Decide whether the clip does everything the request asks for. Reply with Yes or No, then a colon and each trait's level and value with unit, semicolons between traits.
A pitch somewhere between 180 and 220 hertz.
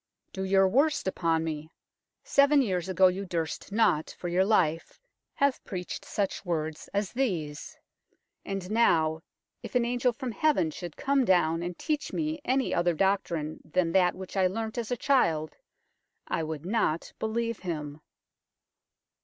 Yes: high, 190 Hz